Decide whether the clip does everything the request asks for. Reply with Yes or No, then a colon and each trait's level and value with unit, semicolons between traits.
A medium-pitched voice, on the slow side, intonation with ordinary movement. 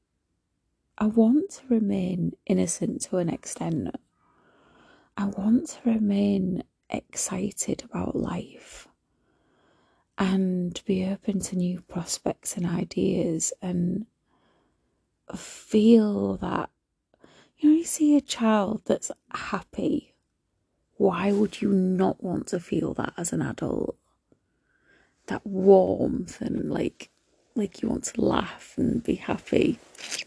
No: high, 200 Hz; slow, 115 wpm; average, 3.4 semitones